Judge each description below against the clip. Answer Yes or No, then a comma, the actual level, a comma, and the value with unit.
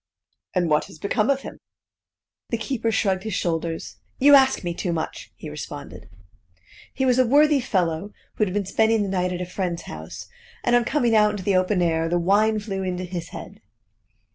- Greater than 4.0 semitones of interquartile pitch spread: Yes, average, 4.4 semitones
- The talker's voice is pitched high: Yes, high, 195 Hz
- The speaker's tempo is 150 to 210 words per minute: Yes, average, 195 wpm